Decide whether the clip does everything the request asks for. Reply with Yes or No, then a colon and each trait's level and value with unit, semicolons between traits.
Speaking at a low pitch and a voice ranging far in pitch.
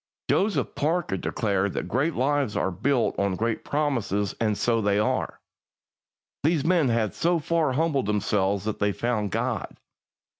Yes: low, 115 Hz; wide, 6.3 semitones